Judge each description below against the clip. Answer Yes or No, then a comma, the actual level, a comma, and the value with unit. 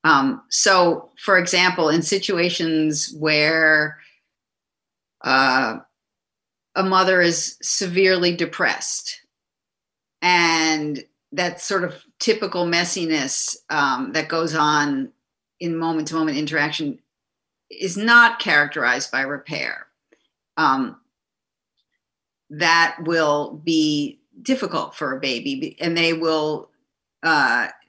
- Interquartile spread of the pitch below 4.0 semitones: Yes, average, 3.5 semitones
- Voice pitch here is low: No, medium, 170 Hz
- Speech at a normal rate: No, slow, 95 wpm